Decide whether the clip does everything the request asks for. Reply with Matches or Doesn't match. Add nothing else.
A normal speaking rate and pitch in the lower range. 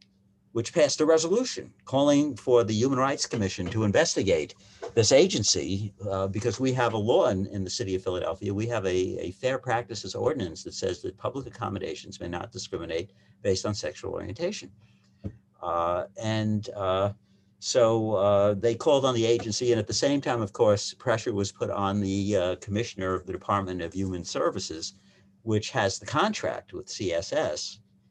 Matches